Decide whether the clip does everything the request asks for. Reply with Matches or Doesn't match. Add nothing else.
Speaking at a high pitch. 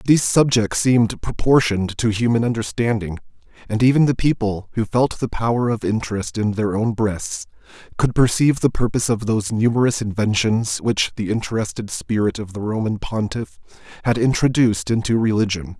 Doesn't match